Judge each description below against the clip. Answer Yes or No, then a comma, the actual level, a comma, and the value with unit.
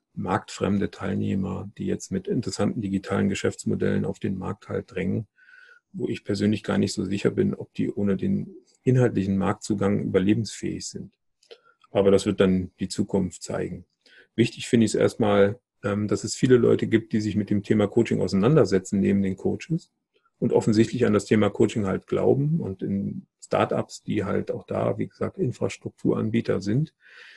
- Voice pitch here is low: Yes, low, 105 Hz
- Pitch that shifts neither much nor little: Yes, average, 3.5 semitones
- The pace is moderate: Yes, average, 165 wpm